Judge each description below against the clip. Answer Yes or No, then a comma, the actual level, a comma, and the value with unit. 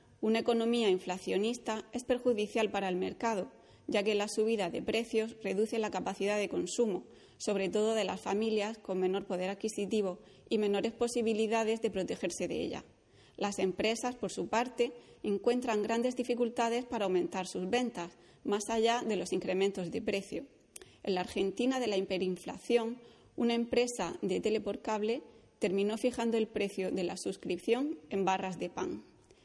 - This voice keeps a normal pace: Yes, average, 155 wpm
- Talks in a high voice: Yes, high, 220 Hz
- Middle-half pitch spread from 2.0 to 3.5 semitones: Yes, average, 3.1 semitones